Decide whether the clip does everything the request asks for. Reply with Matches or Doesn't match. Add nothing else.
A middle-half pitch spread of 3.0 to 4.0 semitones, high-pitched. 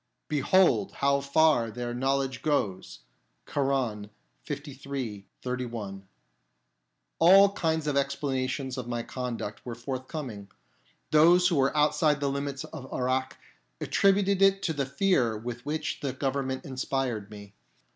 Doesn't match